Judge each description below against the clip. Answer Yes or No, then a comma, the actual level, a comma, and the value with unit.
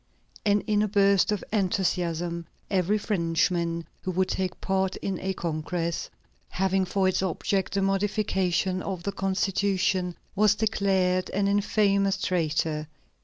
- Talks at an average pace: No, slow, 130 wpm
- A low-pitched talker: No, high, 190 Hz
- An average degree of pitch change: No, narrow, 1.9 semitones